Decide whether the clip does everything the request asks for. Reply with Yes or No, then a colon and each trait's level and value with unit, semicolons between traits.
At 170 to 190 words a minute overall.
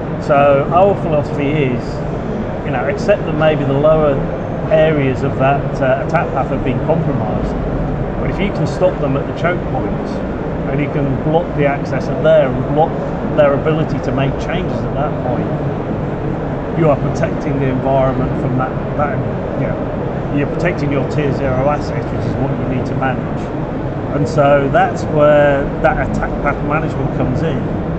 Yes: average, 175 wpm